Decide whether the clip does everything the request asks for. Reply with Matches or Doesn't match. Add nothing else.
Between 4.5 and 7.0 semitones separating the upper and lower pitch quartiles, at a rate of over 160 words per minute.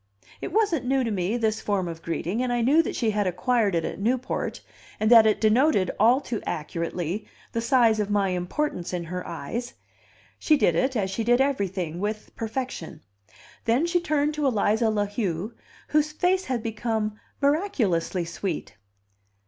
Matches